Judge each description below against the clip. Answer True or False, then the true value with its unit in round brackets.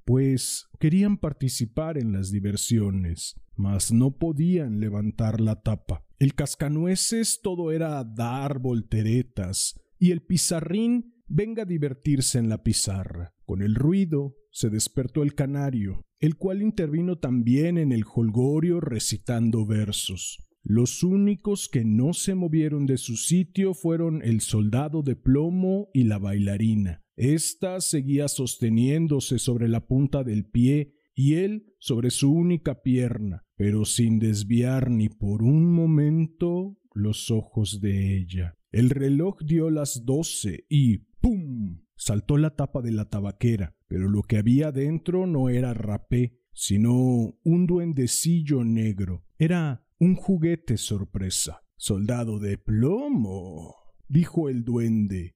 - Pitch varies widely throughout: True (6.7 semitones)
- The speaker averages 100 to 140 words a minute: True (130 wpm)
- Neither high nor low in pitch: False (125 Hz)